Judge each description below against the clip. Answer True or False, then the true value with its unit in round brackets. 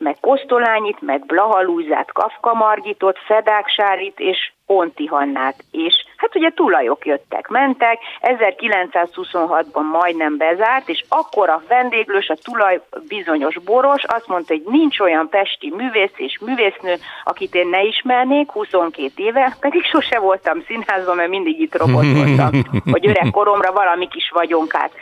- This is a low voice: False (200 Hz)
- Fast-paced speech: False (135 wpm)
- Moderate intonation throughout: False (7.1 semitones)